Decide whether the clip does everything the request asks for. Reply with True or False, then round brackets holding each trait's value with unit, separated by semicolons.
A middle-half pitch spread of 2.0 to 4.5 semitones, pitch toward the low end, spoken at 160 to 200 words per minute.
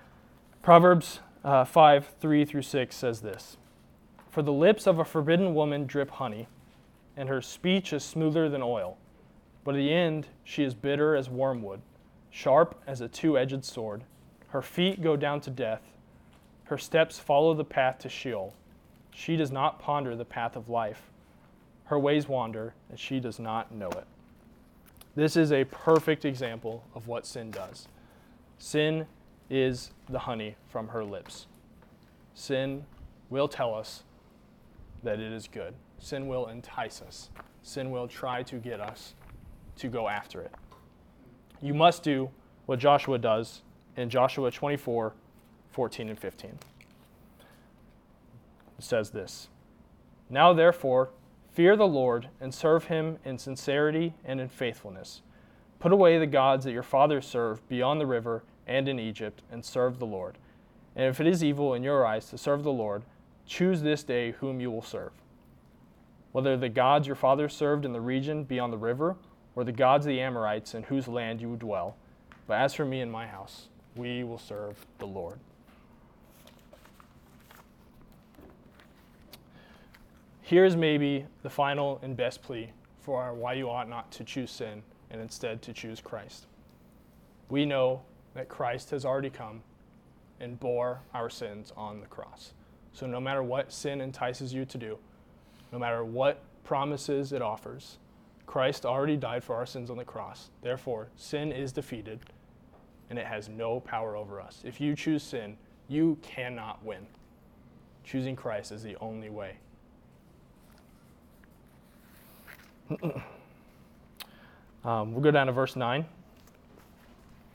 False (3.8 semitones; 130 Hz; 150 wpm)